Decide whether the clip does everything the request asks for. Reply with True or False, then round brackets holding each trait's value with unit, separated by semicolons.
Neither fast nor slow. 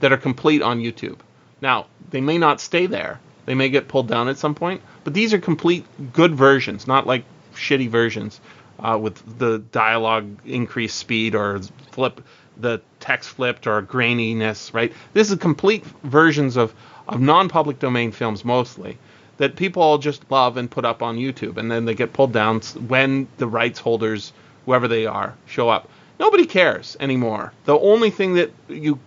True (185 wpm)